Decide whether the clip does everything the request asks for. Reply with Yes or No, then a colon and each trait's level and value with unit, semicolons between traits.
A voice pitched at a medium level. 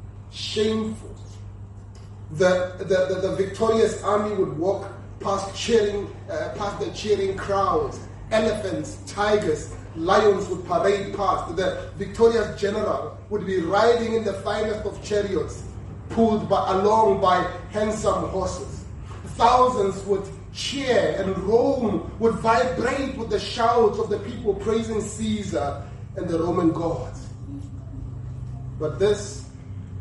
No: high, 195 Hz